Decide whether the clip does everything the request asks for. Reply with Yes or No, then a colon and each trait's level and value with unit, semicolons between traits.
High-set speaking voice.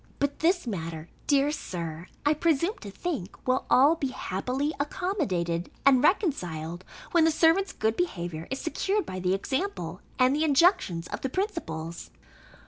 Yes: very high, 265 Hz